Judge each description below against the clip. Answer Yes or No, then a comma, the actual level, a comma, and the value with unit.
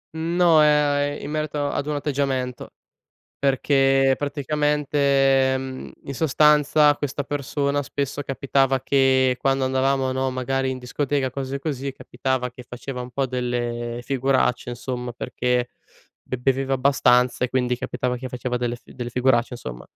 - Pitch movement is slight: Yes, narrow, 2.1 semitones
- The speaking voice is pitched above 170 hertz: No, low, 135 Hz